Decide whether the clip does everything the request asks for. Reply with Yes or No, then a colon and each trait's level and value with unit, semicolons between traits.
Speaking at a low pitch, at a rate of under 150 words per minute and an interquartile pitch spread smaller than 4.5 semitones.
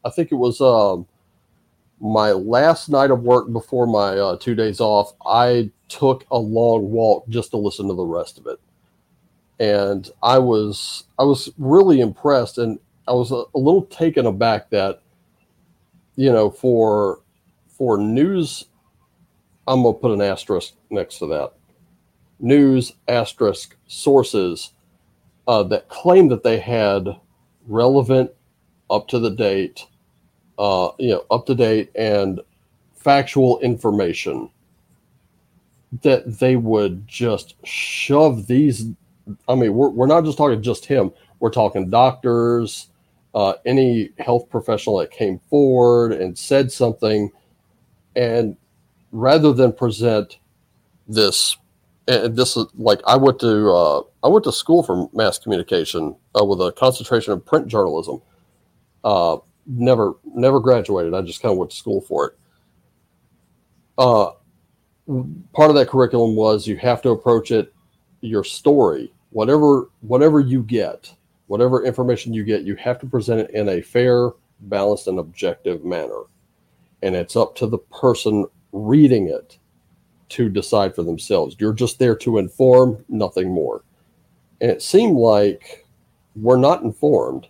Yes: low, 120 Hz; average, 140 wpm; average, 3.5 semitones